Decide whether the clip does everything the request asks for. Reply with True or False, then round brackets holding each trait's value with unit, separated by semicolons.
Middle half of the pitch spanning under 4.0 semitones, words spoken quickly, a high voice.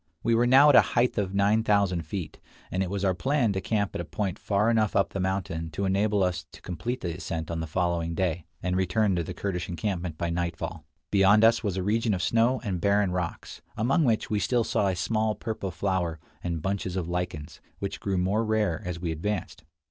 False (3.5 semitones; 225 wpm; 95 Hz)